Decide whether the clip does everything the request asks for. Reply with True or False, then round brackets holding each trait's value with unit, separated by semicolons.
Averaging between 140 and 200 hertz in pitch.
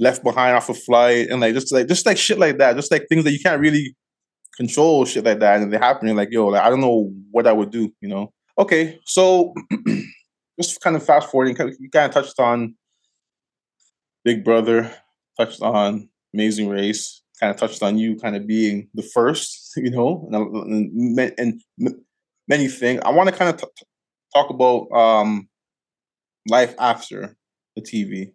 False (120 Hz)